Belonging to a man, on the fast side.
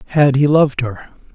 No: male; average, 180 wpm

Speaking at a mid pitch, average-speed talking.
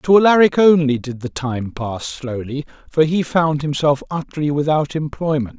Yes: medium, 145 Hz; average, 160 wpm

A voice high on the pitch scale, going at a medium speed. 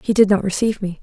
No: high, 200 Hz; fast, 290 wpm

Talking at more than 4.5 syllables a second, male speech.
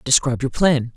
Yes: 5.9 syllables/s; male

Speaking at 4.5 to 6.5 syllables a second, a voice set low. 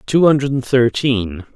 No: 3.7 syllables/s; low, 125 Hz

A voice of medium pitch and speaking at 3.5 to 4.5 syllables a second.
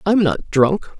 Yes: medium, 180 Hz; 4.4 syllables/s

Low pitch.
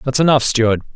Yes: low, 125 Hz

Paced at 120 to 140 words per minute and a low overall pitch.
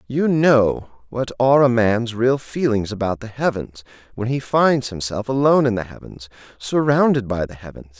No: average, 175 wpm; low, 120 Hz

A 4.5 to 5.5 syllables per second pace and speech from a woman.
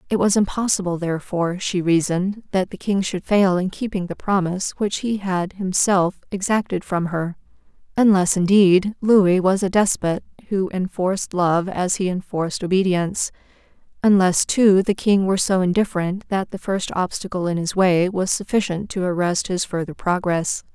Yes: 5.0 syllables/s; female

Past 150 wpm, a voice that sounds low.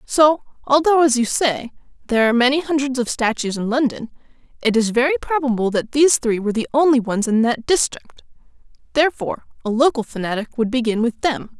No: average, 180 wpm; very high, 255 Hz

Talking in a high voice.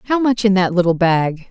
Yes: high, 195 Hz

